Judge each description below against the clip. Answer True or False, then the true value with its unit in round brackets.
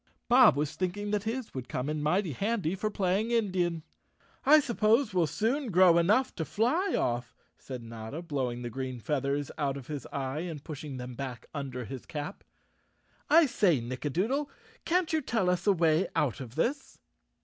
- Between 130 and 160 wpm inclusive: False (180 wpm)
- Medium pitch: True (170 Hz)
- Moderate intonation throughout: False (7.9 semitones)